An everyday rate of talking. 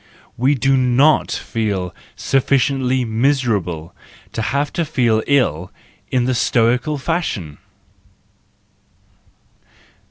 No: slow, 90 wpm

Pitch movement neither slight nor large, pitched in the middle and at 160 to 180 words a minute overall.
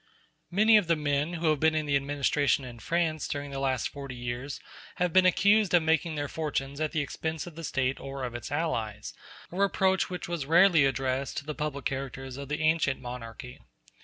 No: average, 3.4 semitones; medium, 145 Hz; fast, 205 wpm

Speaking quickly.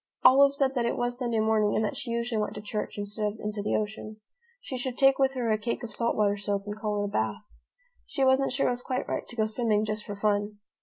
Yes: fast, 265 wpm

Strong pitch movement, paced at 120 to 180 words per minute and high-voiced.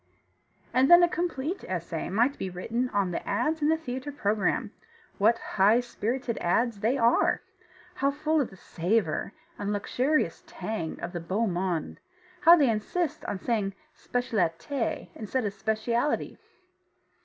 Yes: wide, 5.9 semitones; average, 145 wpm; high, 230 Hz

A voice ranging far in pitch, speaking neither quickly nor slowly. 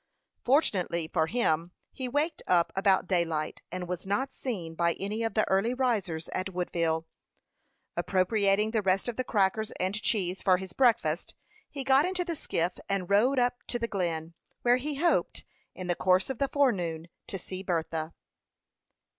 Yes: wide, 5.7 semitones; average, 170 wpm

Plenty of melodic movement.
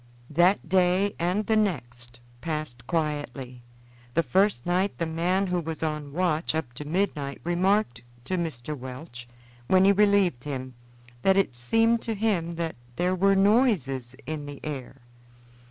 Yes: wide, 5.7 semitones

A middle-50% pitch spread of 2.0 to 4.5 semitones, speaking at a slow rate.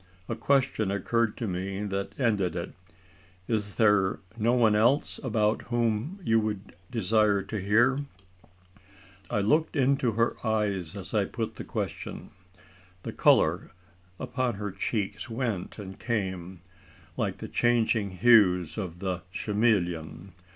Yes: average, 3.4 semitones; slow, 130 wpm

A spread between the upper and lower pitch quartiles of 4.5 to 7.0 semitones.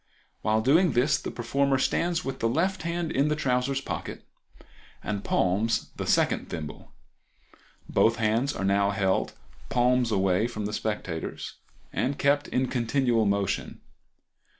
Yes: average, 4.9 semitones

